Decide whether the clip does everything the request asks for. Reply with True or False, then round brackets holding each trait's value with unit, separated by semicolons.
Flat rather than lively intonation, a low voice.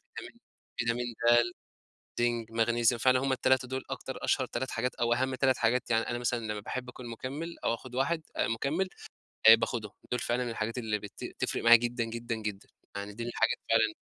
True (2.0 semitones; 120 Hz)